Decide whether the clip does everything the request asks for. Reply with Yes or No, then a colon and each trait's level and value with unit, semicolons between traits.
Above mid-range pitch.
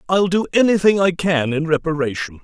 No: medium, 165 Hz